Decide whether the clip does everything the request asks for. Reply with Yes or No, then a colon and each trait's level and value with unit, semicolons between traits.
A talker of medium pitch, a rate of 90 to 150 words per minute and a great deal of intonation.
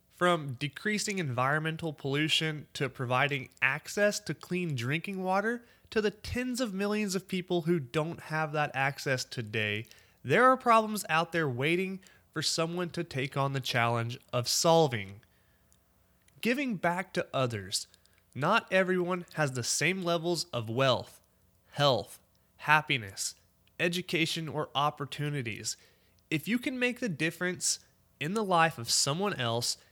Yes: medium, 155 Hz; slow, 135 wpm; wide, 6.1 semitones